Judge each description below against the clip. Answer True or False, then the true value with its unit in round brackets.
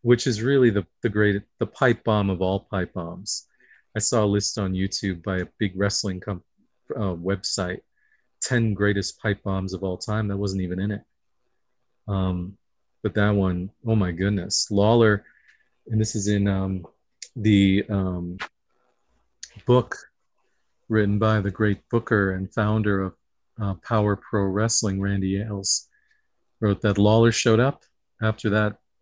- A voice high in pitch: False (100 Hz)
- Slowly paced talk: False (155 wpm)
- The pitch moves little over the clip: True (2.3 semitones)